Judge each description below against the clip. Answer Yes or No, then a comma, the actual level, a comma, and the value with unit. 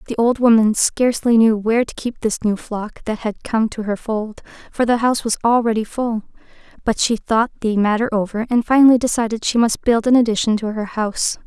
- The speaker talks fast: Yes, fast, 210 wpm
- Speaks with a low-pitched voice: No, high, 225 Hz